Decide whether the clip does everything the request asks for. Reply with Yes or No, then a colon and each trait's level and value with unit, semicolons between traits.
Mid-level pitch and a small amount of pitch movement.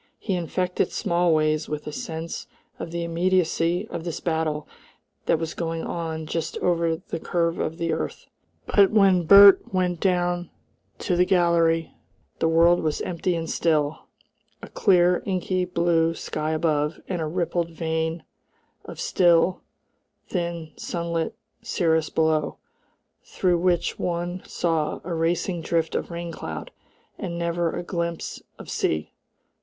Yes: medium, 170 Hz; narrow, 1.5 semitones